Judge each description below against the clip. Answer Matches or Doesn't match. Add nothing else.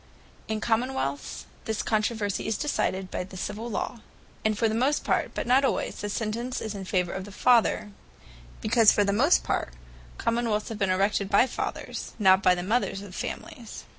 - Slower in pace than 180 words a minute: Doesn't match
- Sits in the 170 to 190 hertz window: Doesn't match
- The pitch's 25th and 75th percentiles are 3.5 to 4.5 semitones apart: Doesn't match